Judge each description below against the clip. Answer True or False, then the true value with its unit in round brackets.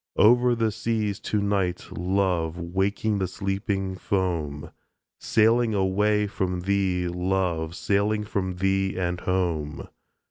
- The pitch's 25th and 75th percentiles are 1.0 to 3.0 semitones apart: True (2.6 semitones)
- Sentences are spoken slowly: True (115 wpm)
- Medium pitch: False (95 Hz)